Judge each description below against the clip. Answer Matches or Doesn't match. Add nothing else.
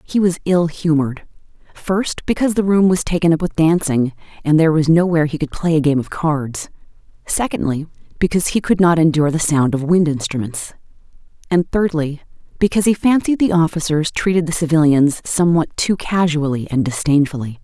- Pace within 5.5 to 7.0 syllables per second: Matches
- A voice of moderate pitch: Matches